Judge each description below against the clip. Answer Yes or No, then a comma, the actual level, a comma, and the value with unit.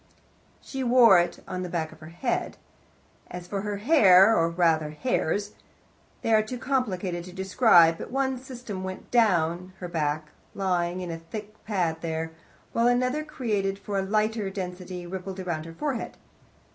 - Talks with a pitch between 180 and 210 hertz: Yes, high, 190 Hz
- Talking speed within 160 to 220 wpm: Yes, average, 165 wpm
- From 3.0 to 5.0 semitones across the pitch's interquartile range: Yes, average, 4.5 semitones